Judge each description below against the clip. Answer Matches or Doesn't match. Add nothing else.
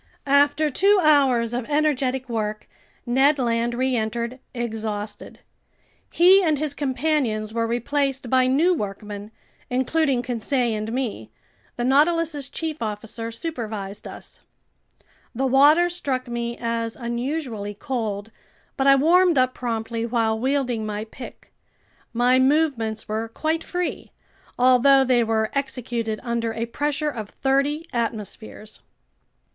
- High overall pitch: Matches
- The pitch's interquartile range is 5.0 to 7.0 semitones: Doesn't match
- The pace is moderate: Doesn't match